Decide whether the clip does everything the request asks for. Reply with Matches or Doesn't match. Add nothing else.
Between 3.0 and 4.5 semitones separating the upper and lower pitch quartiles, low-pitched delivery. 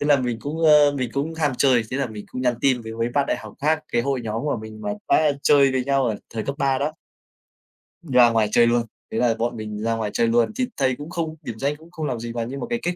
Matches